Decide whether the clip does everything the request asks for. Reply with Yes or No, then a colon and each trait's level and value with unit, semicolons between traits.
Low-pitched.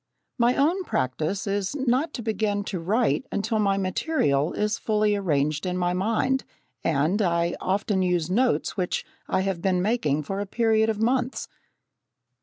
No: high, 200 Hz